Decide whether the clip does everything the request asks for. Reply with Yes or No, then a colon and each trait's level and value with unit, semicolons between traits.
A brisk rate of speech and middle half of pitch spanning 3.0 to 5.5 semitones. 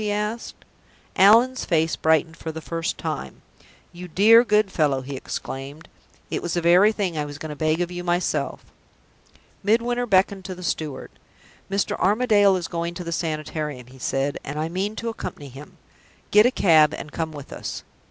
No: average, 180 wpm; average, 4.9 semitones